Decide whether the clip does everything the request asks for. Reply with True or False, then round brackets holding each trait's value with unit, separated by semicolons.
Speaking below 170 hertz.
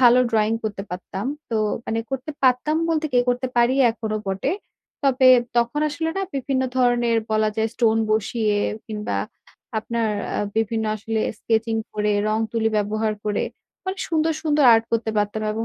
False (225 Hz)